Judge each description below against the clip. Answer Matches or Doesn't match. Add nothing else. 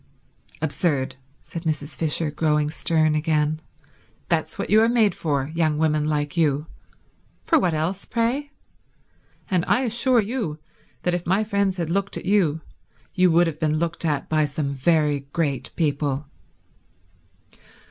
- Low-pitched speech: Doesn't match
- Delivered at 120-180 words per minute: Matches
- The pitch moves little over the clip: Doesn't match